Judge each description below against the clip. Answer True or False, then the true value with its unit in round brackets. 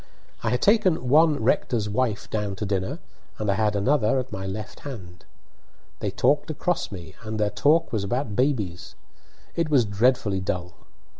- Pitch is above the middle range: False (110 Hz)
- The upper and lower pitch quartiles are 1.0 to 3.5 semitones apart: False (4.8 semitones)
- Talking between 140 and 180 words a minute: True (165 wpm)